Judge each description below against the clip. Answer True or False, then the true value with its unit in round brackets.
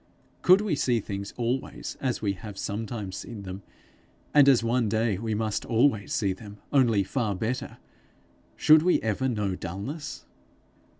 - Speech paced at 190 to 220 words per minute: False (155 wpm)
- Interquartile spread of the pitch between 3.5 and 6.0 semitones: True (4.2 semitones)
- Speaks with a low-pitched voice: True (110 Hz)